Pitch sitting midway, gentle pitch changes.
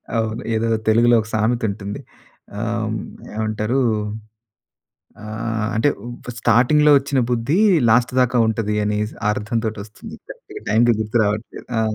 No: low, 115 Hz; narrow, 2.1 semitones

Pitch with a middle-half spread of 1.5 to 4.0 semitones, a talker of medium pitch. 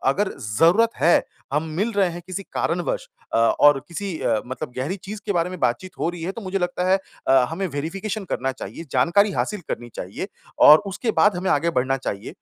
No: wide, 5.6 semitones; medium, 175 Hz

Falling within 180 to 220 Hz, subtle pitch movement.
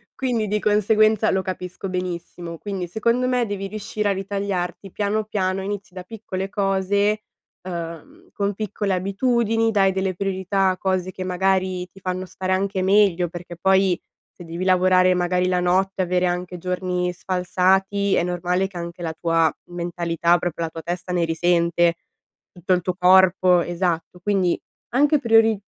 Yes: medium, 185 Hz; narrow, 2.1 semitones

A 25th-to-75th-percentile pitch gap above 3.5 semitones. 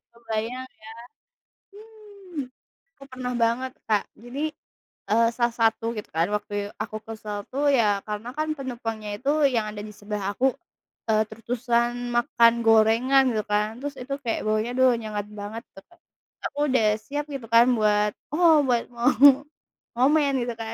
No: average, 3.1 semitones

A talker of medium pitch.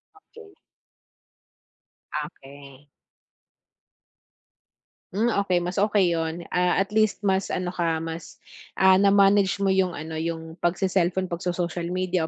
Yes: medium, 180 Hz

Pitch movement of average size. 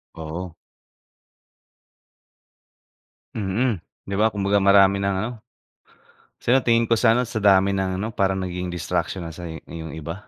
Yes: average, 3.1 semitones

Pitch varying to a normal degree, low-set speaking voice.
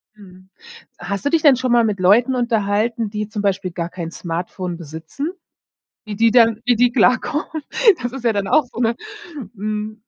No: average, 3.9 semitones; high, 215 Hz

